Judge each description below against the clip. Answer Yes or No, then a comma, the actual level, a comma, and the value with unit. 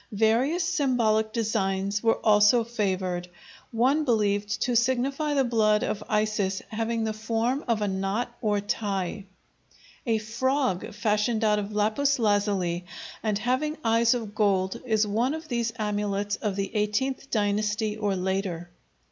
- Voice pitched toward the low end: No, high, 215 Hz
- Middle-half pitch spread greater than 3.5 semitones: No, narrow, 2.6 semitones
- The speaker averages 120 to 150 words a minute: Yes, average, 140 wpm